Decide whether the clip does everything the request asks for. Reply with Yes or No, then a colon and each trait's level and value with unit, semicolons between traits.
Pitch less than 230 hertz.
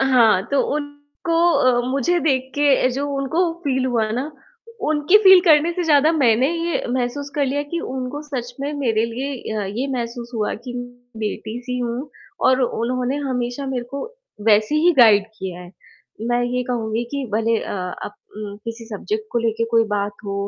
No: very high, 250 Hz